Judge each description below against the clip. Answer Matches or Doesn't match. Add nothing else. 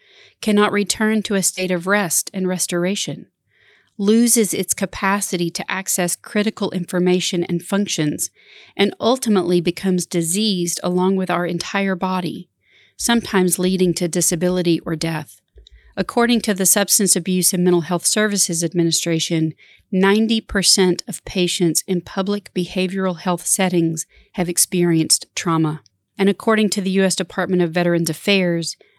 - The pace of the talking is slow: Matches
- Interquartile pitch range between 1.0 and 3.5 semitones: Matches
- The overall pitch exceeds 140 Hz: Matches